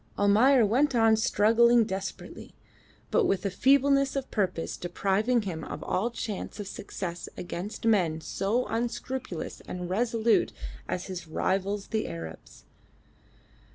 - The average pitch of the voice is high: Yes, high, 210 Hz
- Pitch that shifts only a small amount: No, average, 4.2 semitones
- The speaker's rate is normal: No, slow, 125 wpm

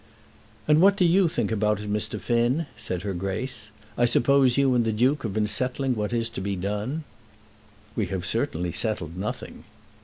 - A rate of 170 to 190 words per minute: Yes, average, 185 wpm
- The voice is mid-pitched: No, low, 115 Hz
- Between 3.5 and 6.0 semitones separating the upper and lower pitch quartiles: Yes, average, 4.4 semitones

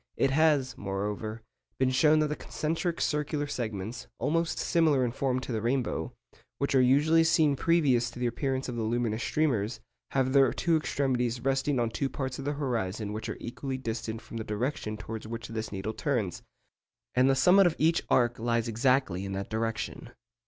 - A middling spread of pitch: Yes, average, 4.1 semitones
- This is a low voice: Yes, low, 125 Hz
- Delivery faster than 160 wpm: Yes, average, 185 wpm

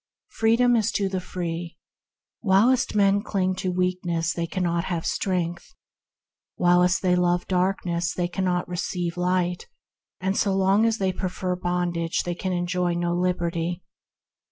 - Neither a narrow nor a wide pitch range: No, narrow, 1.4 semitones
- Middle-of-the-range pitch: Yes, medium, 180 Hz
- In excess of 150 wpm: No, average, 140 wpm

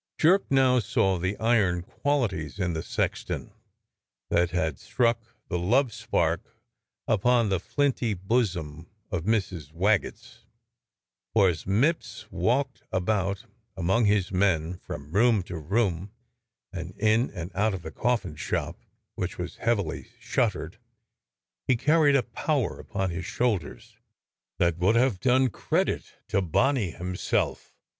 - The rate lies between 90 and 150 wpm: Yes, slow, 135 wpm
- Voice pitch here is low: Yes, low, 100 Hz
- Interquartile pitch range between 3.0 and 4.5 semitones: No, average, 5.2 semitones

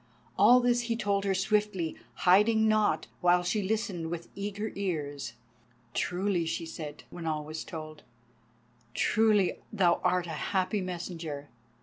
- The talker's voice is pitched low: No, medium, 185 Hz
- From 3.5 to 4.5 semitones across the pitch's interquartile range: Yes, average, 4.2 semitones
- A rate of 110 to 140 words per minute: Yes, slow, 135 wpm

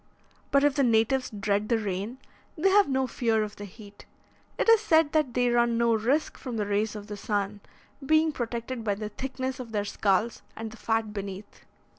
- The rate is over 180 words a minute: Yes, average, 200 wpm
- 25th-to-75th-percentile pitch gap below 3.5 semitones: No, average, 4.0 semitones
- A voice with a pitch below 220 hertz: No, high, 230 Hz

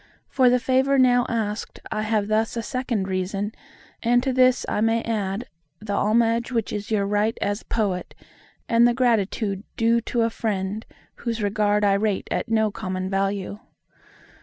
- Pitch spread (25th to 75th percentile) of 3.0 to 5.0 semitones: No, narrow, 2.5 semitones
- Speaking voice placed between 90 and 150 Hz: No, high, 220 Hz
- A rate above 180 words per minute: No, average, 165 wpm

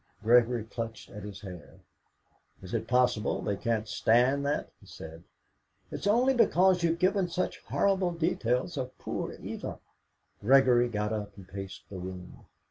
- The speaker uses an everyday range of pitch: No, wide, 8.0 semitones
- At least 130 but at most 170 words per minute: Yes, average, 150 wpm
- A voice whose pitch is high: No, low, 120 Hz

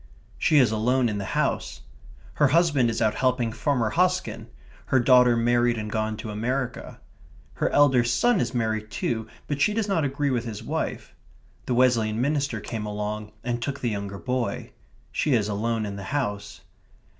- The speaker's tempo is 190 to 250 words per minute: No, average, 175 wpm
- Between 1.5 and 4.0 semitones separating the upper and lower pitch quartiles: Yes, average, 3.7 semitones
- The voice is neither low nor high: No, low, 120 Hz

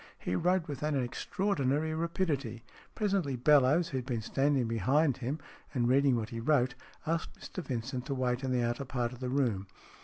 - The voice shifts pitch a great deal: No, average, 3.8 semitones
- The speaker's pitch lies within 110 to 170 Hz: Yes, low, 135 Hz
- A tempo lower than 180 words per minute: No, average, 190 wpm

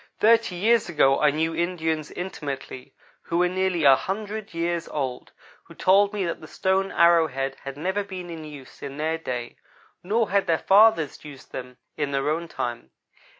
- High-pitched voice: No, medium, 165 Hz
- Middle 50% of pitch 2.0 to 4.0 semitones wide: No, average, 4.8 semitones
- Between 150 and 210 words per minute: Yes, average, 180 wpm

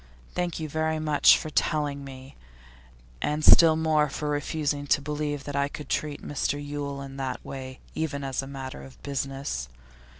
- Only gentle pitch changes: Yes, narrow, 1.9 semitones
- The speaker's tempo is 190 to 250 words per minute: No, average, 170 wpm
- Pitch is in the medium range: Yes, medium, 145 Hz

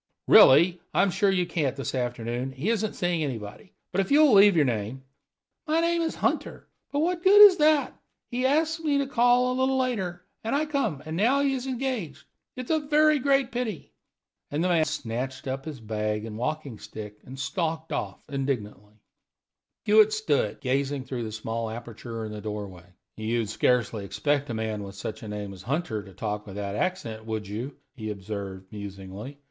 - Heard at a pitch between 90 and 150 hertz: Yes, medium, 140 Hz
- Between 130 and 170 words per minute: No, average, 195 wpm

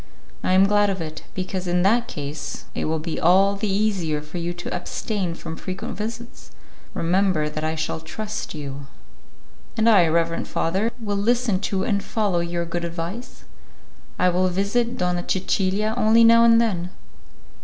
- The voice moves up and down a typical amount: Yes, average, 4.0 semitones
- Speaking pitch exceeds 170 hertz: Yes, medium, 185 Hz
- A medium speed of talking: Yes, average, 165 wpm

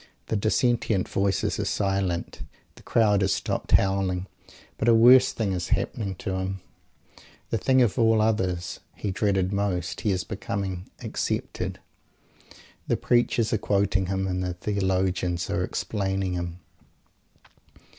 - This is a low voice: Yes, very low, 95 Hz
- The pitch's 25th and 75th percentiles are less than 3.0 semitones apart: Yes, narrow, 2.5 semitones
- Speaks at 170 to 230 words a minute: No, slow, 135 wpm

